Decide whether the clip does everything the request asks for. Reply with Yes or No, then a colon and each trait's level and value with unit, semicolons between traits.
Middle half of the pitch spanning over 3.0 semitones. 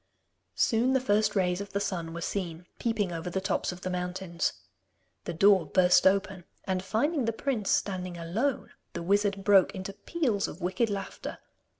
No: narrow, 2.6 semitones